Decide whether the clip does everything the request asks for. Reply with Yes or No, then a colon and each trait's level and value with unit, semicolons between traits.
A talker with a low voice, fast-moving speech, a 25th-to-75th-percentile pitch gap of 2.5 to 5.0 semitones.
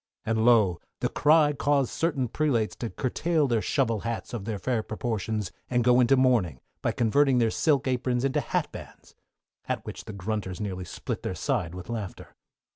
No: low, 120 Hz; average, 175 wpm; average, 3.8 semitones